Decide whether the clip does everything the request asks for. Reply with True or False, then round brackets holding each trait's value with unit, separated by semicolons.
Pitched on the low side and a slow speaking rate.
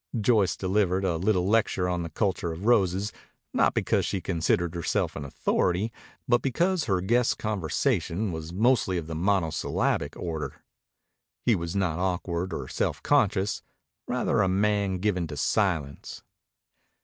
False (95 Hz; 145 wpm)